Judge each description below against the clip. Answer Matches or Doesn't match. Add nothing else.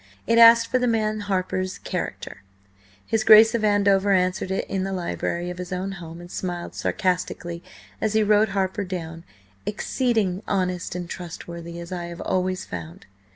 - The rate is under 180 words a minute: Matches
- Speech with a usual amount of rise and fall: Matches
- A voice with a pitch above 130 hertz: Matches